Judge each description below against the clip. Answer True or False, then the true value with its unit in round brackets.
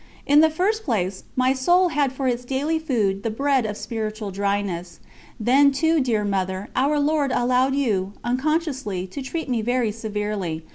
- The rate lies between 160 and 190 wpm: True (165 wpm)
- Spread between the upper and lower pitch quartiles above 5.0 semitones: True (5.5 semitones)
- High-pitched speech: True (250 Hz)